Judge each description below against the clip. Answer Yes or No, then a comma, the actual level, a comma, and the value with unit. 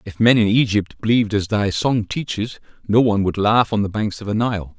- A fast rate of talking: Yes, fast, 240 wpm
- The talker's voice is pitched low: Yes, low, 105 Hz